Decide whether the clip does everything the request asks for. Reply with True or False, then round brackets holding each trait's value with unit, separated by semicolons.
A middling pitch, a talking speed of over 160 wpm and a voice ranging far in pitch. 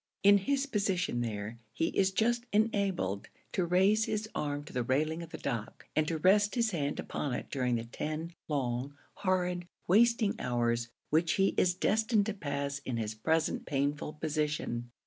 True (160 Hz; 170 wpm; 7.1 semitones)